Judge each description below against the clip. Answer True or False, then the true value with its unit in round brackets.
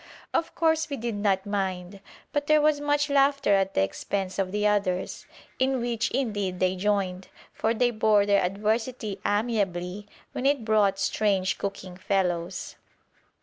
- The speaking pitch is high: True (205 Hz)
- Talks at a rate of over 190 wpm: False (150 wpm)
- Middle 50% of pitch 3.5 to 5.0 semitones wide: True (4.1 semitones)